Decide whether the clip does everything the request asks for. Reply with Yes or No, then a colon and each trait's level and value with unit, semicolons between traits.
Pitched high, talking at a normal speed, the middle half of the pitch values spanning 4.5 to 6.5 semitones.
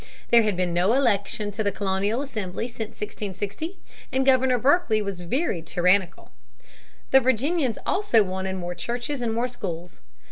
Yes: high, 215 Hz; average, 150 wpm; average, 5.1 semitones